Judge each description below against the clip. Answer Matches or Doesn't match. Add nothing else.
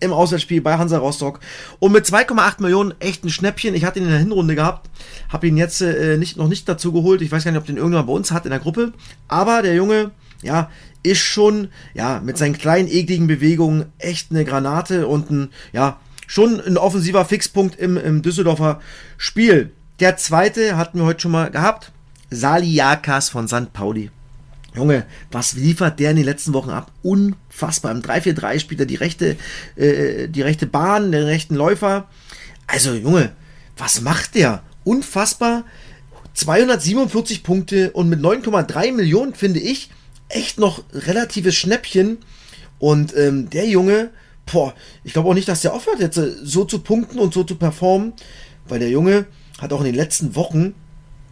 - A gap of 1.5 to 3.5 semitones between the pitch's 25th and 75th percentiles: Doesn't match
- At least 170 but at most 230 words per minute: Matches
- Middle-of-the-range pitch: Matches